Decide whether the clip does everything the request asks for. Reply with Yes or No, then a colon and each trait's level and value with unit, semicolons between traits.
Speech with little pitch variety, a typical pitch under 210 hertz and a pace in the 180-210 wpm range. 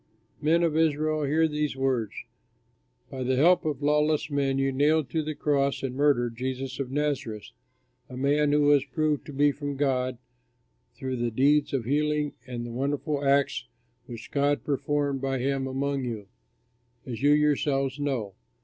No: narrow, 2.2 semitones; medium, 140 Hz; average, 165 wpm